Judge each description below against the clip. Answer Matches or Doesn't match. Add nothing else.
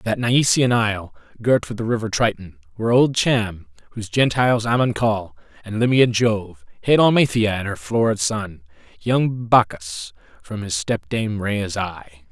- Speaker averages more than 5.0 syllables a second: Doesn't match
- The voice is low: Matches